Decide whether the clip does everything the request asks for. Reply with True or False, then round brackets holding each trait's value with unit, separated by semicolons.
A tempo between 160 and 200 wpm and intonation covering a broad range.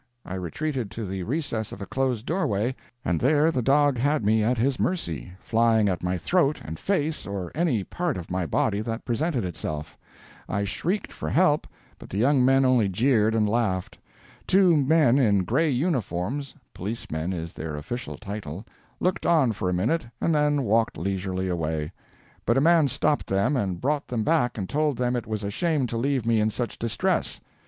True (190 wpm; 6.9 semitones)